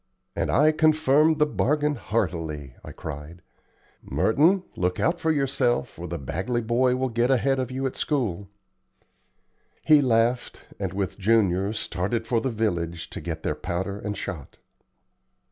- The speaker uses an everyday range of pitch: No, wide, 7.1 semitones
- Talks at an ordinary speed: Yes, average, 150 wpm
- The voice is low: Yes, low, 115 Hz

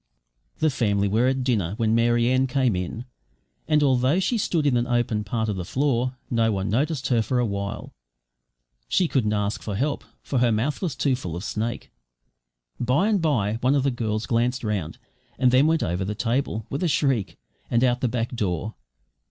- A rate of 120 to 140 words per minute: No, average, 200 wpm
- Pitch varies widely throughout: No, average, 3.8 semitones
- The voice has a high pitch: No, low, 120 Hz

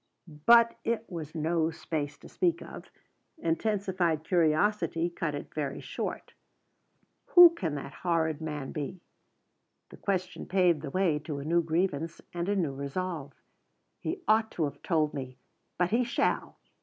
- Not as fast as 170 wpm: Yes, average, 150 wpm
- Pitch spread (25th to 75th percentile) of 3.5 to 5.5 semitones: Yes, average, 3.8 semitones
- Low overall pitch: No, medium, 165 Hz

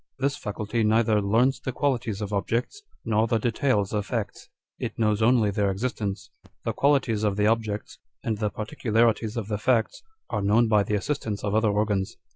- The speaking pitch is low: Yes, low, 110 Hz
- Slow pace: No, average, 180 wpm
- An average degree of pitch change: No, narrow, 2.2 semitones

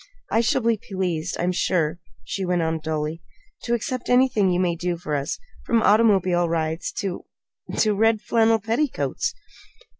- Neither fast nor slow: Yes, average, 155 wpm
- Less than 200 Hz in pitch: Yes, medium, 185 Hz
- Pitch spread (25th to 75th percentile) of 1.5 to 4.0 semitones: No, average, 5.0 semitones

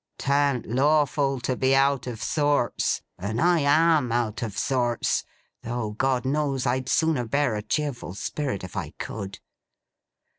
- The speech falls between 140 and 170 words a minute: Yes, average, 145 wpm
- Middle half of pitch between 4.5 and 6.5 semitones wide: No, average, 3.4 semitones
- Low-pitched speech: Yes, low, 130 Hz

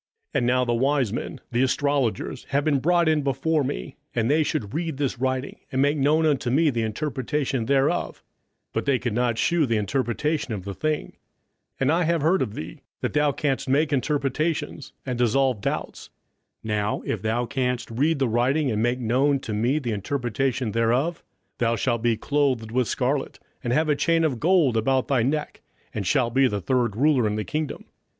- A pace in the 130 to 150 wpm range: No, average, 195 wpm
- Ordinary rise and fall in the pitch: Yes, average, 3.8 semitones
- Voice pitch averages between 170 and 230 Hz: No, low, 130 Hz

